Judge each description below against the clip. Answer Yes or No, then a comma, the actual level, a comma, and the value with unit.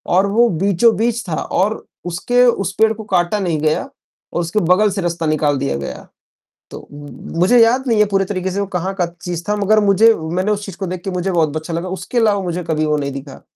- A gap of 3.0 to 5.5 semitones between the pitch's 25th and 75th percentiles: Yes, average, 3.8 semitones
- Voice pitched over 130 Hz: Yes, high, 190 Hz